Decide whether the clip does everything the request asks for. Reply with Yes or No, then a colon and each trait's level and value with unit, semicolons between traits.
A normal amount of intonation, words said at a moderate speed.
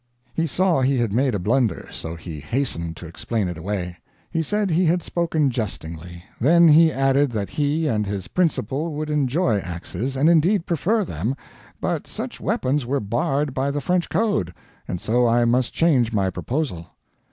No: wide, 7.8 semitones; average, 175 wpm